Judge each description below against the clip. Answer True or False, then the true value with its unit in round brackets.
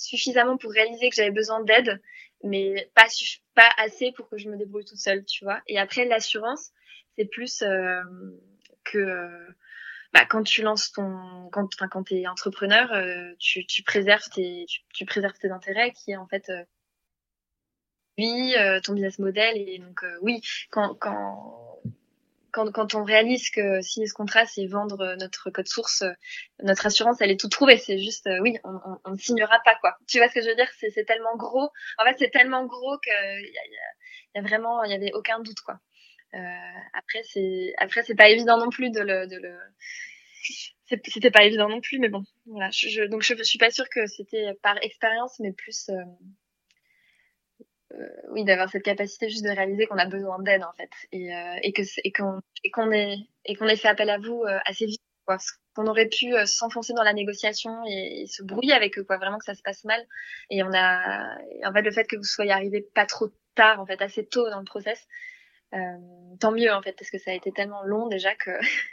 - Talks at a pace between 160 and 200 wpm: False (210 wpm)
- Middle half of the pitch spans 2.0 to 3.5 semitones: True (2.8 semitones)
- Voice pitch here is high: True (210 Hz)